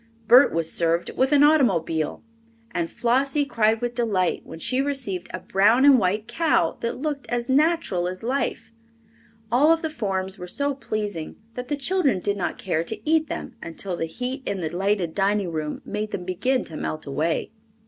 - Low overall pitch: No, high, 215 Hz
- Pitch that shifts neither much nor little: No, wide, 7.0 semitones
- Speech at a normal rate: Yes, average, 185 wpm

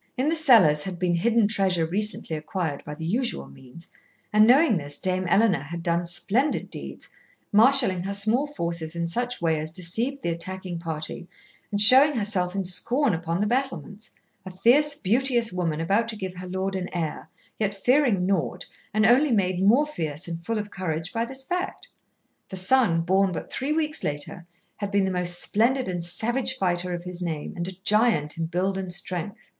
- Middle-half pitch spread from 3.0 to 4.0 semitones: No, average, 5.2 semitones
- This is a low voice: No, high, 190 Hz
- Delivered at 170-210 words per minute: Yes, average, 190 wpm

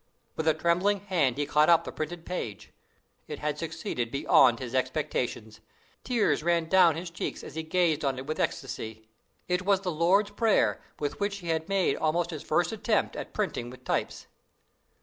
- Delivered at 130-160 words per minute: No, average, 185 wpm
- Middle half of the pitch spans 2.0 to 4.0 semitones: No, average, 4.7 semitones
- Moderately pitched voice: Yes, medium, 160 Hz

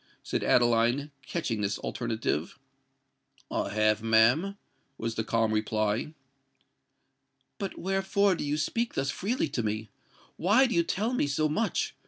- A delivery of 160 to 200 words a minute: No, average, 145 wpm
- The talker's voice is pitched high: No, low, 135 Hz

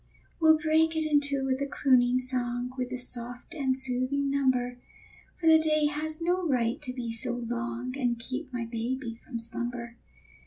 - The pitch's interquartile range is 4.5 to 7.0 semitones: No, average, 3.1 semitones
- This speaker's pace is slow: No, average, 180 wpm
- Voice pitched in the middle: No, very high, 255 Hz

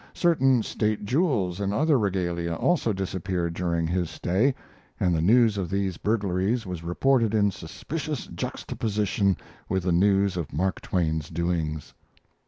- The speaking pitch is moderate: No, very low, 95 Hz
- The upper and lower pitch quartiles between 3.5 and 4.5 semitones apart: Yes, average, 4.1 semitones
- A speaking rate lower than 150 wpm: Yes, average, 140 wpm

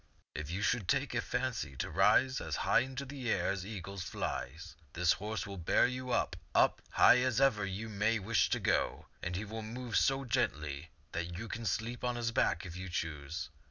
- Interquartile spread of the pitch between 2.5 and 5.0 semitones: No, wide, 5.4 semitones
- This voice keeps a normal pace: No, fast, 215 wpm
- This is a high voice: No, low, 100 Hz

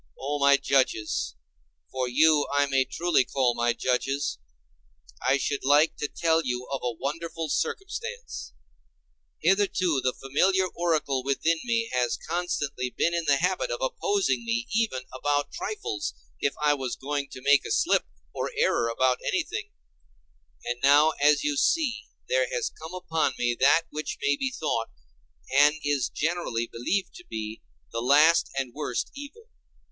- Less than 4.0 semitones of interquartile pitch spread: No, average, 5.2 semitones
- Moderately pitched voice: Yes, medium, 145 Hz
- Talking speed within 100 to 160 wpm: Yes, average, 150 wpm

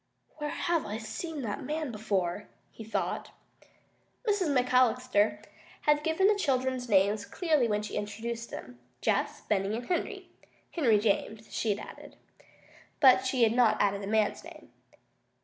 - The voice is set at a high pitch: Yes, high, 230 Hz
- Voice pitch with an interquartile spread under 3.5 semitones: No, average, 4.9 semitones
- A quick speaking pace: No, average, 150 wpm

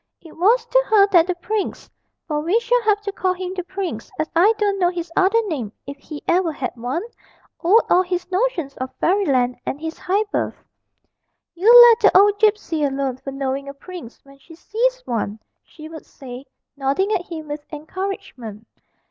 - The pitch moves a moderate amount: No, wide, 6.2 semitones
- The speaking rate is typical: Yes, average, 190 wpm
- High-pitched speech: Yes, very high, 345 Hz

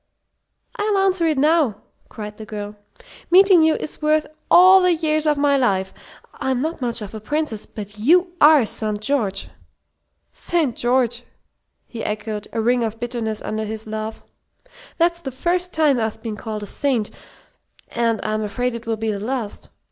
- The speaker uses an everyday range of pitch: No, wide, 6.2 semitones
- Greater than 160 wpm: Yes, average, 170 wpm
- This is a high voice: Yes, high, 240 Hz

